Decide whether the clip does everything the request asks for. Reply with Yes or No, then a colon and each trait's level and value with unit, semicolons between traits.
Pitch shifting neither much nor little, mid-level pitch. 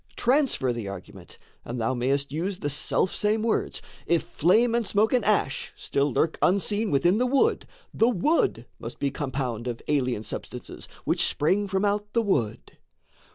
No: wide, 8.0 semitones; medium, 175 Hz